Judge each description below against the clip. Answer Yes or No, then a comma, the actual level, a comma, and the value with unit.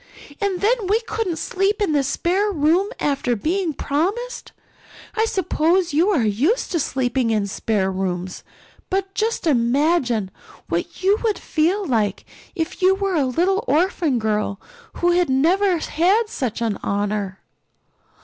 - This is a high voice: Yes, very high, 325 Hz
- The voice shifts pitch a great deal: Yes, wide, 8.4 semitones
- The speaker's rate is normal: Yes, average, 145 wpm